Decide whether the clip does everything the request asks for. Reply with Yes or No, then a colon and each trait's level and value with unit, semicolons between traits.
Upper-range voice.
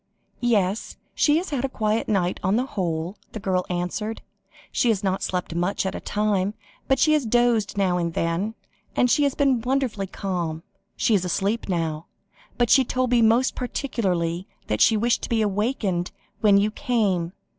Yes: high, 210 Hz